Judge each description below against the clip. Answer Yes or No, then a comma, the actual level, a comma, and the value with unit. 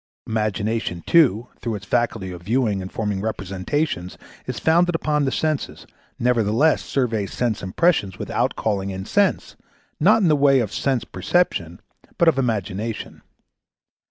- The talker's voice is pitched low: Yes, low, 115 Hz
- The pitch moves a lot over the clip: Yes, wide, 6.6 semitones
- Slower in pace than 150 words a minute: Yes, average, 140 wpm